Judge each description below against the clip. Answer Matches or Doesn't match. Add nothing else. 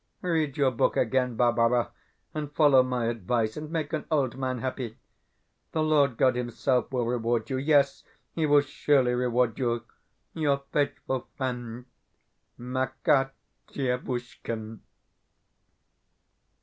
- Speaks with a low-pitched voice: Matches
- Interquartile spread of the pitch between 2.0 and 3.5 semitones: Matches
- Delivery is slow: Matches